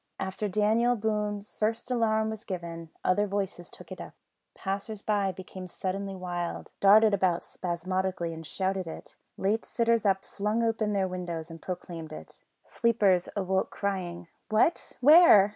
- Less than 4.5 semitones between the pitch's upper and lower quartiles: Yes, average, 3.0 semitones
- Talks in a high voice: Yes, high, 195 Hz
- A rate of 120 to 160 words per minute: Yes, average, 145 wpm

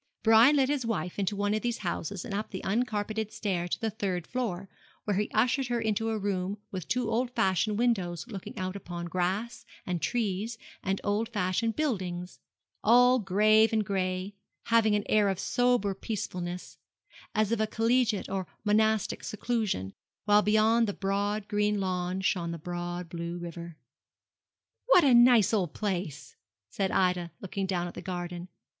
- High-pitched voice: Yes, high, 205 Hz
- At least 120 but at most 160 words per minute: No, average, 170 wpm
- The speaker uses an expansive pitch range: No, average, 3.5 semitones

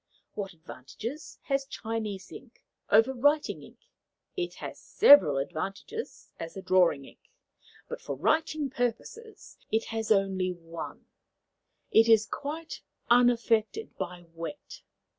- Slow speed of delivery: Yes, slow, 120 wpm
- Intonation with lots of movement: Yes, wide, 7.2 semitones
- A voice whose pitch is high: Yes, high, 225 Hz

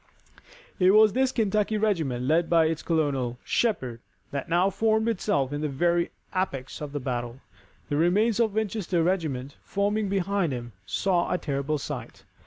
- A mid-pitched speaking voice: Yes, medium, 170 Hz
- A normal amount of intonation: No, wide, 6.3 semitones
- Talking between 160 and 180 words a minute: Yes, average, 165 wpm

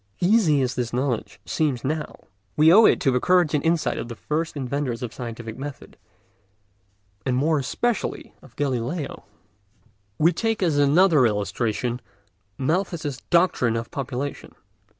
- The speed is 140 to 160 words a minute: Yes, average, 145 wpm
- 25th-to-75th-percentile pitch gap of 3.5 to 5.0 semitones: Yes, average, 4.7 semitones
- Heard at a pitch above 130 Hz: Yes, medium, 140 Hz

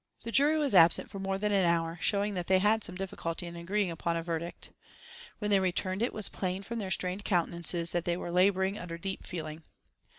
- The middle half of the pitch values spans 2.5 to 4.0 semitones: Yes, average, 2.8 semitones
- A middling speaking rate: No, fast, 220 wpm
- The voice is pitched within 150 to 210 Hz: Yes, medium, 185 Hz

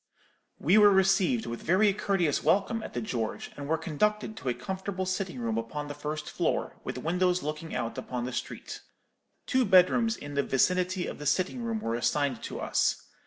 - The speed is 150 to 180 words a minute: No, average, 190 wpm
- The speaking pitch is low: No, medium, 175 Hz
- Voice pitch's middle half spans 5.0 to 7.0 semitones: Yes, wide, 5.6 semitones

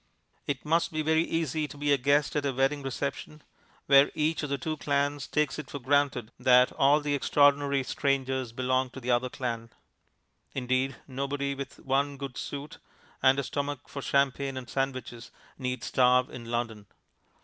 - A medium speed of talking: Yes, average, 170 wpm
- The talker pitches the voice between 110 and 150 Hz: Yes, medium, 140 Hz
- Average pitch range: No, narrow, 2.0 semitones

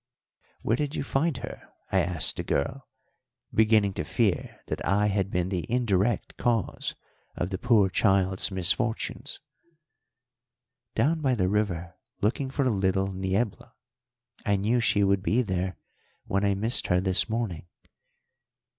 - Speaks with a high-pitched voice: No, low, 100 Hz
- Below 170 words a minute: Yes, average, 140 wpm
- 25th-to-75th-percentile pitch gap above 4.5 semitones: No, average, 3.9 semitones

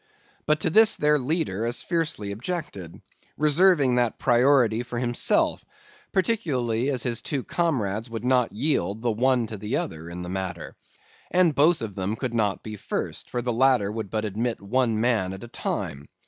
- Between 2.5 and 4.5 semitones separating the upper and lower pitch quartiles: No, average, 4.9 semitones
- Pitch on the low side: Yes, low, 120 Hz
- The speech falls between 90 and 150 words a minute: No, average, 175 wpm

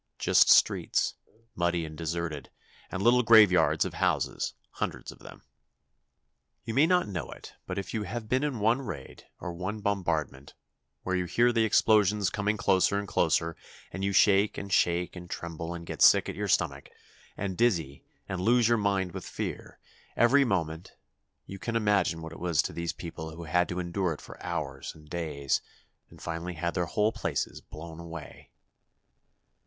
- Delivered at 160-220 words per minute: Yes, average, 175 wpm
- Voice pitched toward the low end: Yes, very low, 90 Hz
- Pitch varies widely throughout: No, average, 4.0 semitones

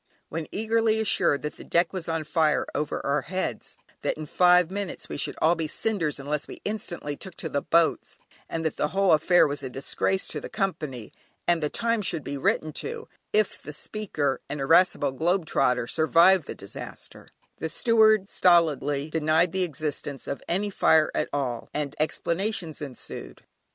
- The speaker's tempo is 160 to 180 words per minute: Yes, average, 175 wpm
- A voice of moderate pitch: Yes, medium, 160 Hz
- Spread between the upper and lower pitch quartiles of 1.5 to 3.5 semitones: No, average, 4.4 semitones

